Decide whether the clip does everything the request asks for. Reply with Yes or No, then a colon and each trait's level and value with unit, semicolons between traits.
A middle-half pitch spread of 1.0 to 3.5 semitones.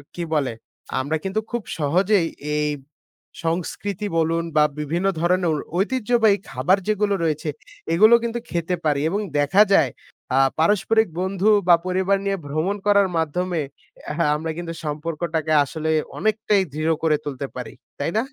No: average, 4.3 semitones